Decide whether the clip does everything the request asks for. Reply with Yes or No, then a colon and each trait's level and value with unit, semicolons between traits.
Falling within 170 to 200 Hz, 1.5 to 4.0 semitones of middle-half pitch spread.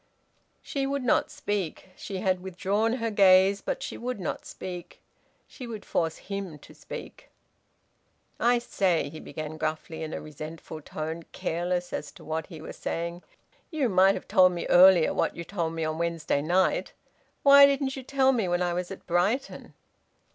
No: medium, 185 Hz; average, 5.0 semitones